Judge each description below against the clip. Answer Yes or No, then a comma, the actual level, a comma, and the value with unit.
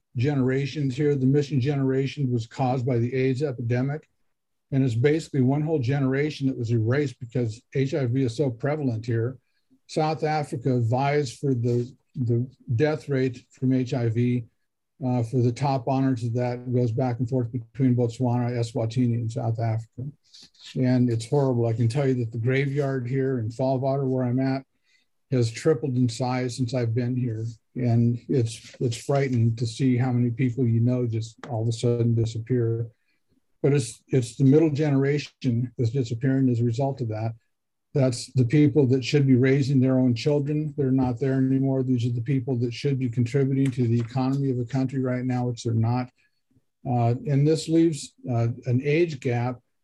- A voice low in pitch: Yes, low, 130 Hz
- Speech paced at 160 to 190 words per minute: Yes, average, 180 wpm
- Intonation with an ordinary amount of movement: No, narrow, 2.0 semitones